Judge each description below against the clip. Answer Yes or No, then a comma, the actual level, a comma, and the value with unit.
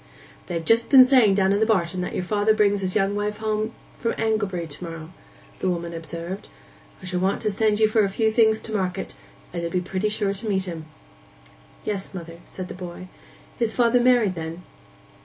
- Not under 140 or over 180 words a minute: No, average, 200 wpm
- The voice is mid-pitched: No, high, 195 Hz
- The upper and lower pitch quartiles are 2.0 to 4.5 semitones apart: Yes, average, 3.4 semitones